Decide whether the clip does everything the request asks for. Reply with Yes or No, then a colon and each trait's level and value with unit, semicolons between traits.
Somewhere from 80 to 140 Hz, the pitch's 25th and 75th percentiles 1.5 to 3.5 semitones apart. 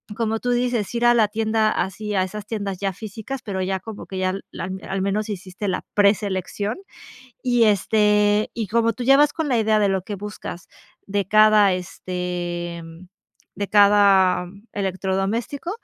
No: high, 205 Hz; narrow, 2.5 semitones